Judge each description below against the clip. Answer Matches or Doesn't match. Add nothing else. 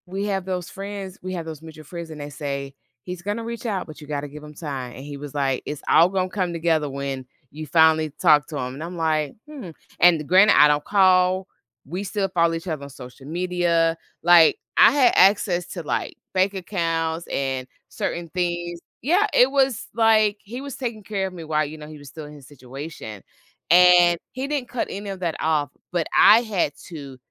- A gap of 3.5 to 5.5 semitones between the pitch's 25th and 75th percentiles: Matches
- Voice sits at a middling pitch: Matches